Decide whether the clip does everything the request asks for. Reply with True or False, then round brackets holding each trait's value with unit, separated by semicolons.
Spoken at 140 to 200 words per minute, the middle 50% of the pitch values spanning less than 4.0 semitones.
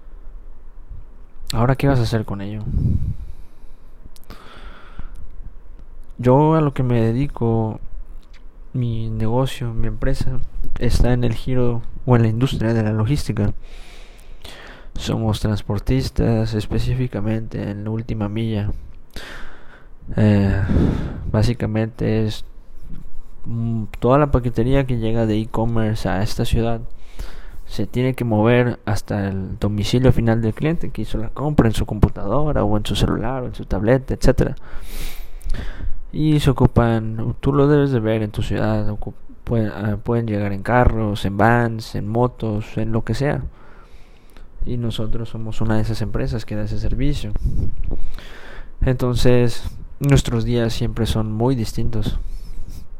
False (130 wpm; 2.7 semitones)